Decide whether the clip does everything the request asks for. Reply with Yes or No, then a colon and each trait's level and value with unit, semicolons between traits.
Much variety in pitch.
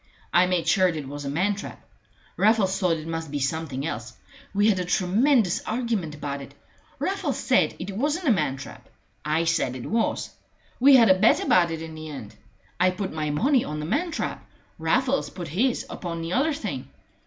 Yes: wide, 6.4 semitones